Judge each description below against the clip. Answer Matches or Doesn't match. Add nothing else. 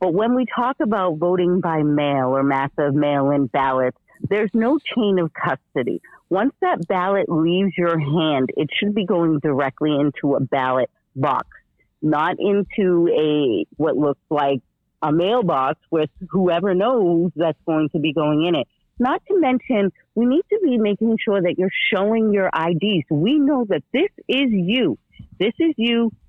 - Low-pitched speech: Doesn't match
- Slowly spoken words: Doesn't match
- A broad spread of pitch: Matches